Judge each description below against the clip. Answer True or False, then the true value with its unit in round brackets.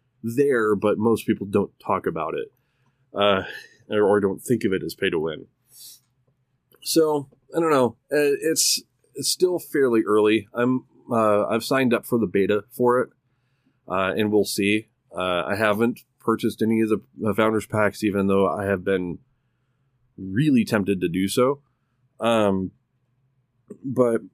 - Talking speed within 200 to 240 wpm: False (155 wpm)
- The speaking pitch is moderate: False (120 Hz)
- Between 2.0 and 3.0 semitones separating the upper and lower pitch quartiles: False (3.8 semitones)